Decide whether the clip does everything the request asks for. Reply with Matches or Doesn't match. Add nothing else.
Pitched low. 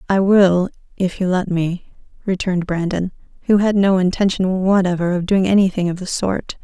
Doesn't match